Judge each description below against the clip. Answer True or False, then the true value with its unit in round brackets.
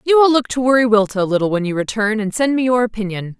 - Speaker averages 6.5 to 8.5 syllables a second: True (6.7 syllables/s)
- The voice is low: False (225 Hz)